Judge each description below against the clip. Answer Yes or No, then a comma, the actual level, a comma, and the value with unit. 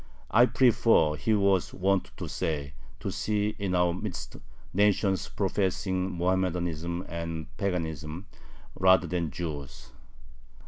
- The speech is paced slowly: Yes, slow, 110 wpm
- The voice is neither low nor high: No, very low, 90 Hz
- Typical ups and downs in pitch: Yes, average, 3.0 semitones